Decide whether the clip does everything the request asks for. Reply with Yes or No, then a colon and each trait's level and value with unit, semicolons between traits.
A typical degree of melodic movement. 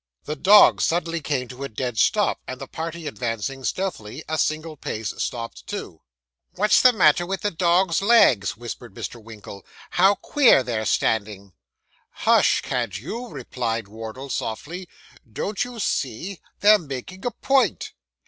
No: wide, 8.3 semitones